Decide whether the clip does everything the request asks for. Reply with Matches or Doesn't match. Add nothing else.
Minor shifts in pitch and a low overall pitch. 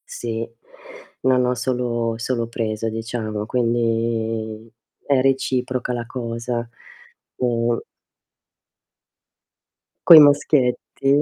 Matches